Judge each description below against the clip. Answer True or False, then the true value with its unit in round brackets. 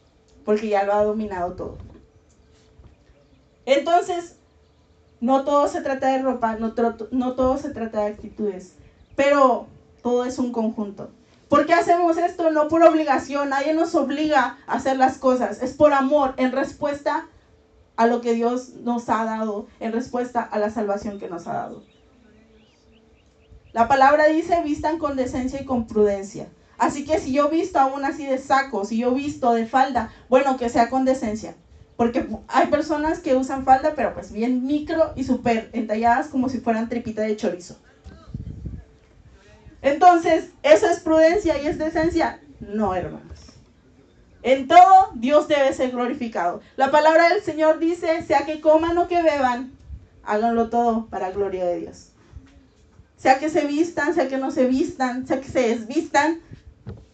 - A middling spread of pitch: True (4.6 semitones)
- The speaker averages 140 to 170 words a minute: True (160 wpm)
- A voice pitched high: True (265 Hz)